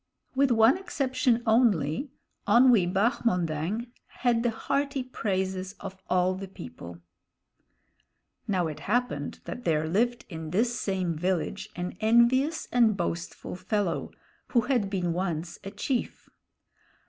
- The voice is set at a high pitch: Yes, high, 200 Hz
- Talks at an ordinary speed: No, slow, 125 wpm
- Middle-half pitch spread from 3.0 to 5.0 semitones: No, wide, 5.4 semitones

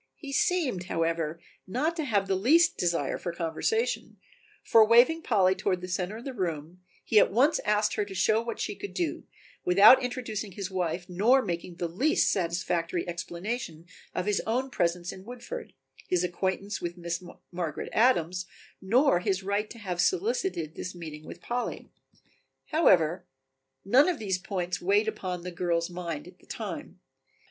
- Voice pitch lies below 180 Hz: No, high, 190 Hz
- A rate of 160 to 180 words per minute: Yes, average, 165 wpm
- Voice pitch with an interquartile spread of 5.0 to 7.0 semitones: Yes, average, 5.3 semitones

